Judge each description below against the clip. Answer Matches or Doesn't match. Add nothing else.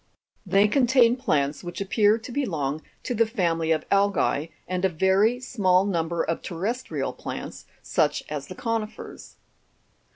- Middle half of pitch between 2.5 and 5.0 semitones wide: Doesn't match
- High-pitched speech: Matches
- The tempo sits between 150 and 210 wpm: Doesn't match